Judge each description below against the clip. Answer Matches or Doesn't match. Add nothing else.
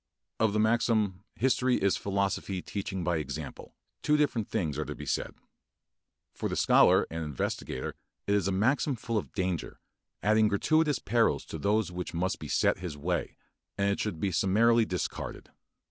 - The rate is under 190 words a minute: Matches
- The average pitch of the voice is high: Doesn't match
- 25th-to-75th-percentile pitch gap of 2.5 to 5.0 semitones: Matches